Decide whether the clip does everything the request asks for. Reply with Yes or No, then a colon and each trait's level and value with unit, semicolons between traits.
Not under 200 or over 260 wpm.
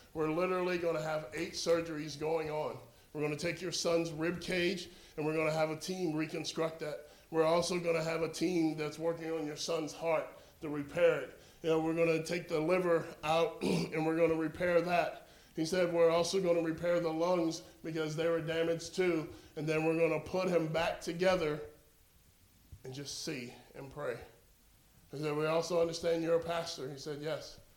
Yes: fast, 205 wpm